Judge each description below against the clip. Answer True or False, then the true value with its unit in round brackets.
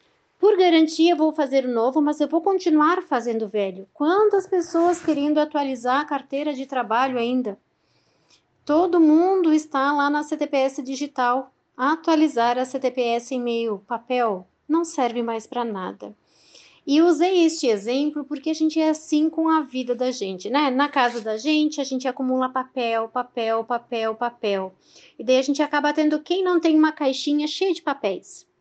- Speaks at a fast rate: False (170 wpm)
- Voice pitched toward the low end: False (280 Hz)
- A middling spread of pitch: True (4.2 semitones)